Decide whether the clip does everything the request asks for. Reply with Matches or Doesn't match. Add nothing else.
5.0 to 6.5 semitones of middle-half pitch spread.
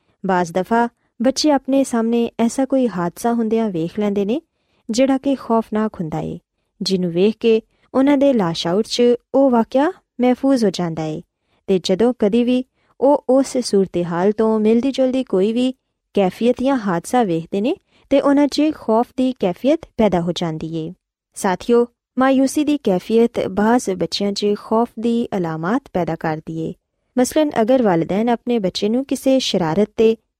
Matches